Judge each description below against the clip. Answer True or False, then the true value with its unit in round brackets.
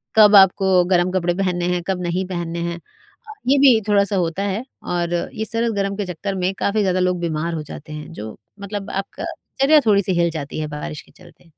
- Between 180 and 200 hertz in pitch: True (185 Hz)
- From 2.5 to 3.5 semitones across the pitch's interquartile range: True (2.8 semitones)